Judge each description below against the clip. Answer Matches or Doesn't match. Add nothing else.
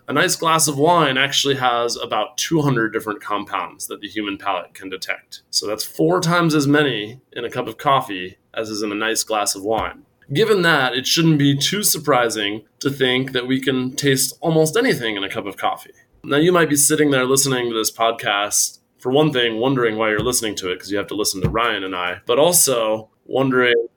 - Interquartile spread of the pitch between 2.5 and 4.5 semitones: Doesn't match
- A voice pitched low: Matches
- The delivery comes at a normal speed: Doesn't match